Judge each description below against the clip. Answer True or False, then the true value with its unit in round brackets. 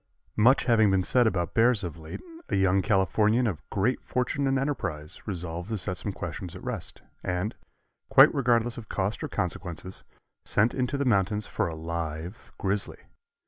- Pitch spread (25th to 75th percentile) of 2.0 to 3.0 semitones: False (4.8 semitones)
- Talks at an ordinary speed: True (170 wpm)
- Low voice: True (100 Hz)